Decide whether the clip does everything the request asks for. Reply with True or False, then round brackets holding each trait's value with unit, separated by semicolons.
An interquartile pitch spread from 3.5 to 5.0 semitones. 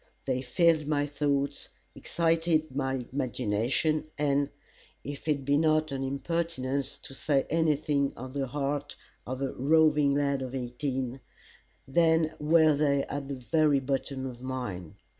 False (2.6 semitones)